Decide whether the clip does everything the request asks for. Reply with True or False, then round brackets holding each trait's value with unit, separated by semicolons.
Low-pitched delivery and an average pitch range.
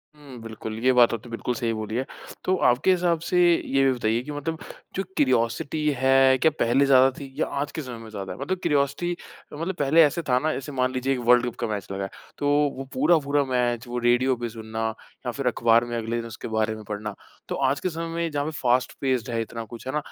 True (130 Hz; 3.7 semitones)